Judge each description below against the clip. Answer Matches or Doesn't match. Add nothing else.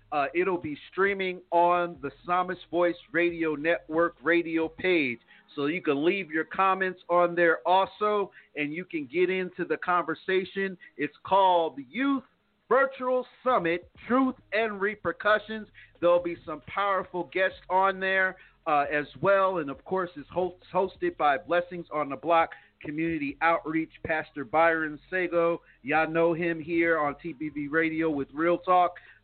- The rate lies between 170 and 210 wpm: Doesn't match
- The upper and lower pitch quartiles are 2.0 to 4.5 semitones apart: Matches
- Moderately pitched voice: Matches